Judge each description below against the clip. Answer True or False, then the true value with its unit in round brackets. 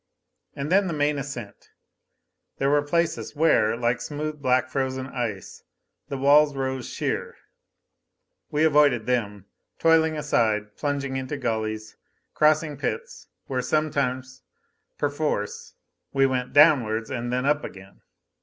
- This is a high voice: False (135 Hz)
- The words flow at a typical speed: False (125 wpm)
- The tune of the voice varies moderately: True (3.6 semitones)